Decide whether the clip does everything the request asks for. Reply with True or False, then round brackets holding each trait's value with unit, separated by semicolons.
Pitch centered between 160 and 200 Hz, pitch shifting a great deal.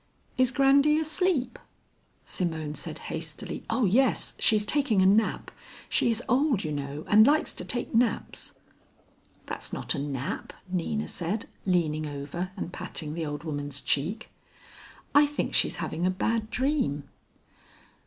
True (190 Hz; 8.6 semitones)